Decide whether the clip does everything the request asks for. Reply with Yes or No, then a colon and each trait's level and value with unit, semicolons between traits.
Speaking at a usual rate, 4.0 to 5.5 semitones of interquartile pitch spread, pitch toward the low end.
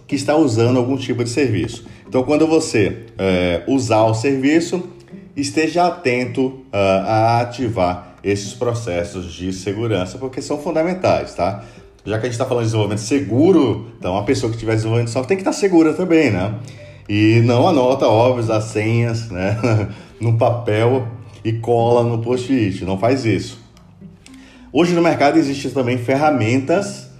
Yes: average, 160 wpm; average, 4.5 semitones; low, 120 Hz